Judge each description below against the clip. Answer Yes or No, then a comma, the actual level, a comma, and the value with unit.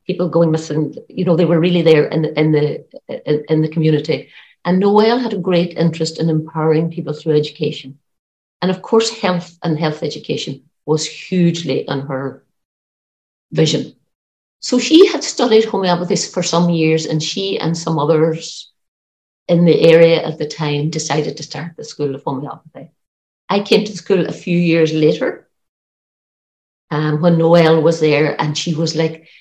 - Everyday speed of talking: Yes, average, 165 wpm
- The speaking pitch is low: No, medium, 160 Hz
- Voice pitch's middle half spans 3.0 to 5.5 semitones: No, narrow, 2.4 semitones